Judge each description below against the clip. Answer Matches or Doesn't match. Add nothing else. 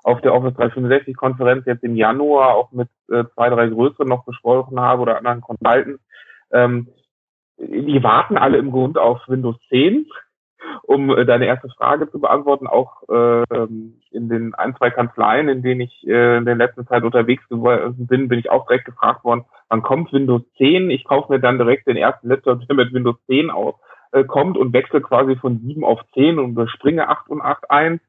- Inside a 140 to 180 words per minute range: Doesn't match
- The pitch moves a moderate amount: Doesn't match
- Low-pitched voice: Matches